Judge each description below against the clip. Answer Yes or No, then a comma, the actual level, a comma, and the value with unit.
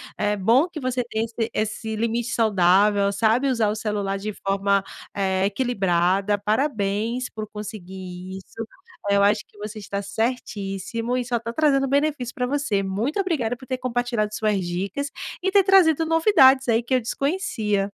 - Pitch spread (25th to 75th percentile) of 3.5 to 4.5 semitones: Yes, average, 4.2 semitones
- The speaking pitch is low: No, high, 220 Hz